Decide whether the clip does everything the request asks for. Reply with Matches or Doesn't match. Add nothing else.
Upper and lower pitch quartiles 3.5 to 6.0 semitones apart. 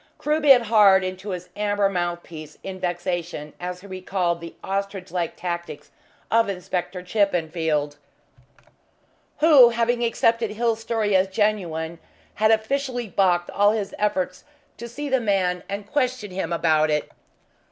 Matches